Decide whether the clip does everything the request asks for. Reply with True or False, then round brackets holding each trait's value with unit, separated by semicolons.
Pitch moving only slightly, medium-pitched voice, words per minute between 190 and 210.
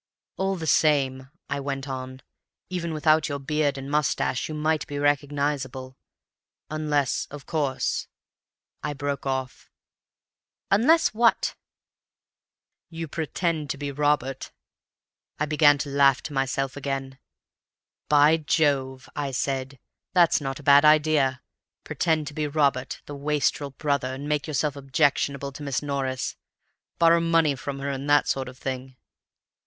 False (2.1 semitones; 145 Hz; 140 wpm)